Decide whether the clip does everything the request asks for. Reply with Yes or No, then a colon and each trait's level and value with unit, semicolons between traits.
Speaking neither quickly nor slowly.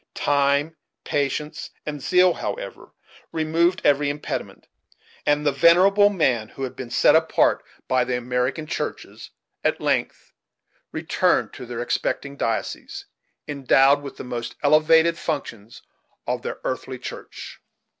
No: slow, 125 wpm